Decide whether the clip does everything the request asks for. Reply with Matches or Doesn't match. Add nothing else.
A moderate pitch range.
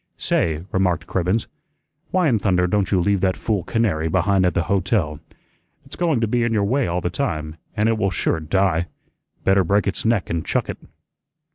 Matches